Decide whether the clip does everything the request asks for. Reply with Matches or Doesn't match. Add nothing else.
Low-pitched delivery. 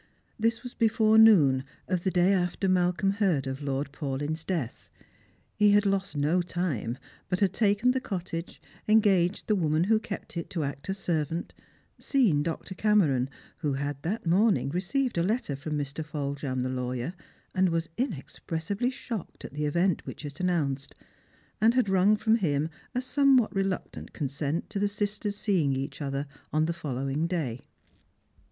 Doesn't match